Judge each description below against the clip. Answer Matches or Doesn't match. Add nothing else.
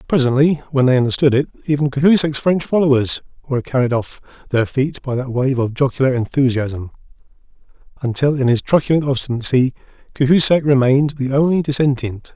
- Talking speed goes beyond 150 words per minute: Doesn't match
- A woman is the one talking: Doesn't match